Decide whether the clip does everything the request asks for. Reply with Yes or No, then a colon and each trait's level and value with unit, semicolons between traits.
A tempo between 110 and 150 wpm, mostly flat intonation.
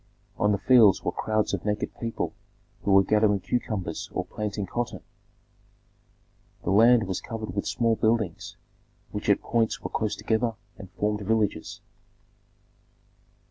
Yes: average, 140 wpm; narrow, 2.1 semitones